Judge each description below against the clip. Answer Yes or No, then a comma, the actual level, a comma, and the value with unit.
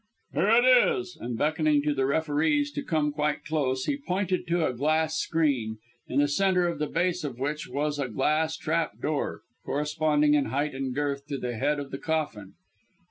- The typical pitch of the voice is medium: Yes, medium, 150 Hz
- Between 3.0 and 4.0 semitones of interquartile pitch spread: No, narrow, 2.6 semitones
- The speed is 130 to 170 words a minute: No, average, 190 wpm